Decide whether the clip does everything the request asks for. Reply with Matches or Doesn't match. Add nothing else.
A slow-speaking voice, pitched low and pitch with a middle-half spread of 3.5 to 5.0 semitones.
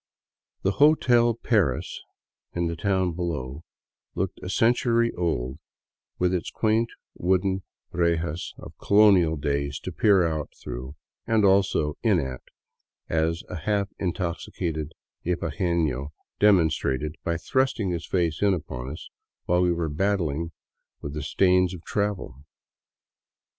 Matches